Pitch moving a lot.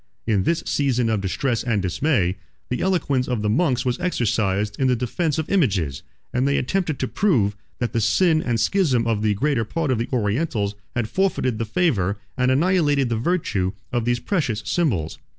Yes: wide, 6.0 semitones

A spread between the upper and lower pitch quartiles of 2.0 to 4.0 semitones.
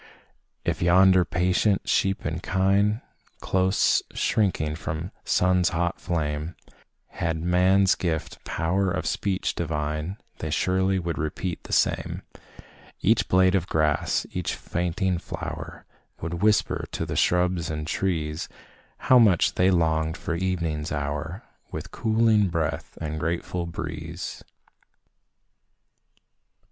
Yes: average, 2.8 semitones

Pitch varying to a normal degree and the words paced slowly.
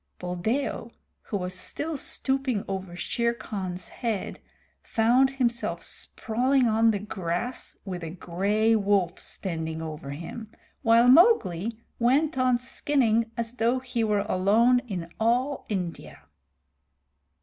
Yes: average, 5.0 semitones; slow, 120 wpm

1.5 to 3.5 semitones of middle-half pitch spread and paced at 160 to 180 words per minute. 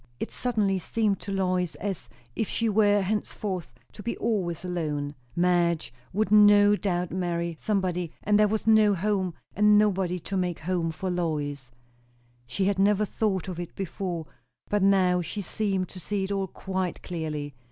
Yes: average, 3.0 semitones; average, 165 wpm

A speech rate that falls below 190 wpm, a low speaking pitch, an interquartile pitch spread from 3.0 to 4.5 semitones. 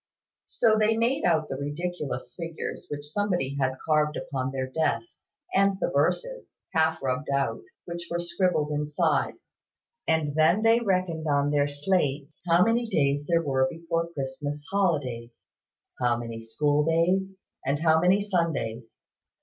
No: average, 150 wpm; medium, 155 Hz; average, 4.1 semitones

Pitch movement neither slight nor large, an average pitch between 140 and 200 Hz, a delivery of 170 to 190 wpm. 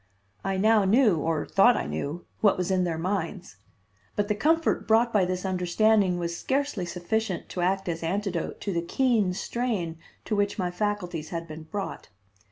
Yes: average, 3.7 semitones; high, 190 Hz; average, 175 wpm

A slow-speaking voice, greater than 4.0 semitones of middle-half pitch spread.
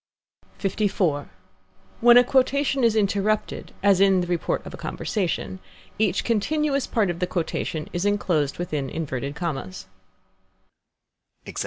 Yes: slow, 125 wpm; average, 4.8 semitones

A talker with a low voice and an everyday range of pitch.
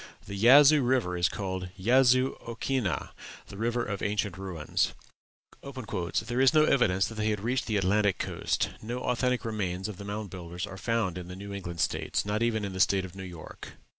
Yes: low, 105 Hz; average, 4.3 semitones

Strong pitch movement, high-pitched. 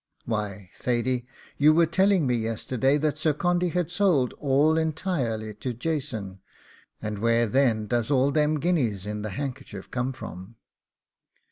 No: wide, 5.9 semitones; low, 130 Hz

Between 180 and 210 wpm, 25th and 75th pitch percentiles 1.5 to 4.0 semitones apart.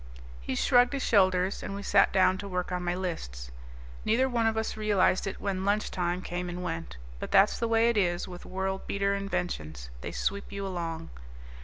Yes: average, 200 wpm; narrow, 2.4 semitones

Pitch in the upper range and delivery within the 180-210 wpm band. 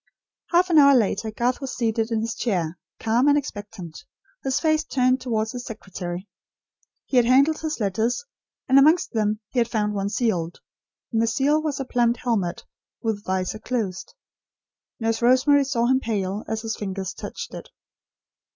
No: high, 230 Hz; average, 170 wpm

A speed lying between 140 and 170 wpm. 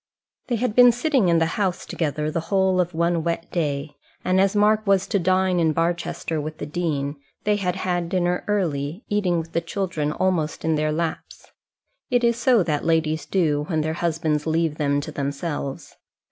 No: average, 190 wpm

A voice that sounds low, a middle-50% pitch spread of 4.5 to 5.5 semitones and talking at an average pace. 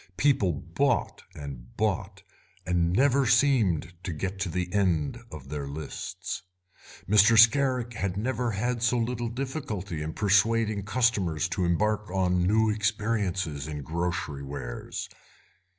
No: low, 100 Hz; average, 5.1 semitones; slow, 130 wpm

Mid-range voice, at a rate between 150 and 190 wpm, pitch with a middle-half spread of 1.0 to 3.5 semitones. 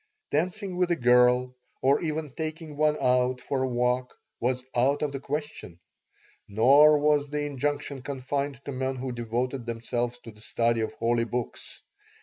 No: low, 130 Hz; average, 160 wpm; average, 3.1 semitones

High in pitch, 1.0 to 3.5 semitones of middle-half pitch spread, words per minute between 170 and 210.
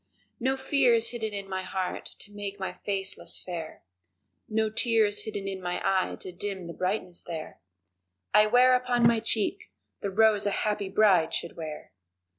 Yes: high, 205 Hz; average, 2.9 semitones; average, 180 wpm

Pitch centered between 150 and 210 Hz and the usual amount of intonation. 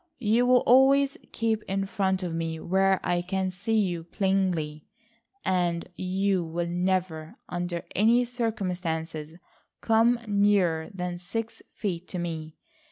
Yes: medium, 185 Hz; average, 3.4 semitones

